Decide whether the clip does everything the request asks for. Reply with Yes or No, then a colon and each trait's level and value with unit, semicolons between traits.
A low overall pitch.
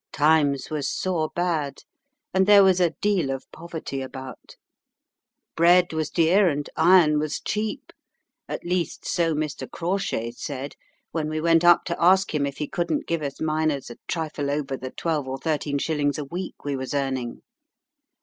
No: medium, 155 Hz